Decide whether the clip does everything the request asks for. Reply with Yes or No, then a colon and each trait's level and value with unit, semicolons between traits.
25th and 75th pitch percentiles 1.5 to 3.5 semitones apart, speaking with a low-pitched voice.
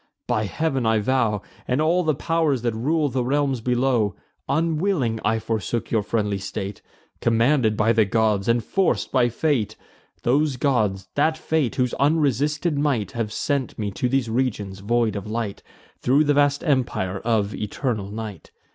No: average, 4.9 semitones; low, 120 Hz